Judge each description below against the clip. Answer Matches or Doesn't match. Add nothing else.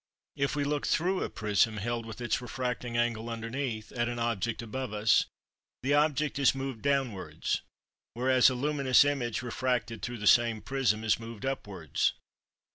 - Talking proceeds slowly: Doesn't match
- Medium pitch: Doesn't match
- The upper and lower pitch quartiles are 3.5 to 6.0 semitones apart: Doesn't match